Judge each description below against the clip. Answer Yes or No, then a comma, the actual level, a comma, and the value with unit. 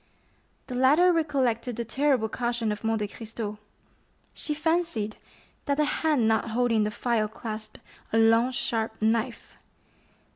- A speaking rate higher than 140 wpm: No, slow, 135 wpm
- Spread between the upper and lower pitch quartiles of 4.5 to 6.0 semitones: No, average, 3.3 semitones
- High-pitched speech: Yes, high, 230 Hz